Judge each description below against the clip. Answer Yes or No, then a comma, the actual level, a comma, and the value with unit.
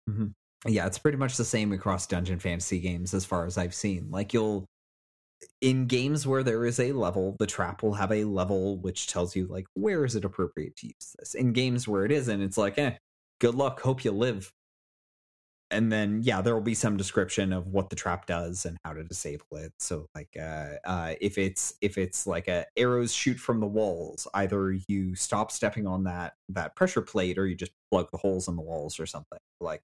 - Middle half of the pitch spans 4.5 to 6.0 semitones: No, average, 3.8 semitones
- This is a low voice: Yes, very low, 95 Hz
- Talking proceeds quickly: Yes, fast, 220 wpm